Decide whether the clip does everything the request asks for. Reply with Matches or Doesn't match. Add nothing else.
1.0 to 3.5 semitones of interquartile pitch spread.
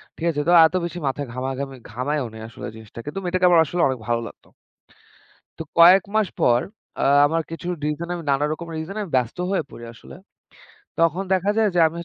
Doesn't match